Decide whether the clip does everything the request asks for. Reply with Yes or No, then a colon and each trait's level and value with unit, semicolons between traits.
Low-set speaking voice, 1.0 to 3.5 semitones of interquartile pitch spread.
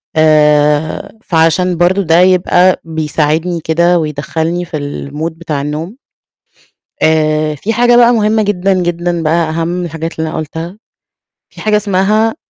No: medium, 165 Hz; average, 2.7 semitones